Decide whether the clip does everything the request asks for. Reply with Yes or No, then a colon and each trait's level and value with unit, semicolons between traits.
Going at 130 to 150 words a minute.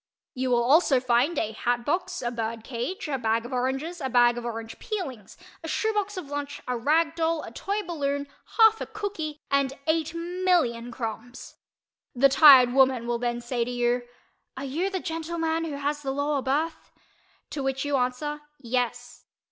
No: average, 180 wpm